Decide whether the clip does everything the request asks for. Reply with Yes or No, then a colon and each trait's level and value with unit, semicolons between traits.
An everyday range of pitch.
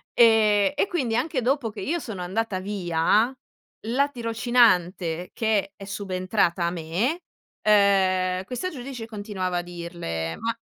Yes: average, 4.4 semitones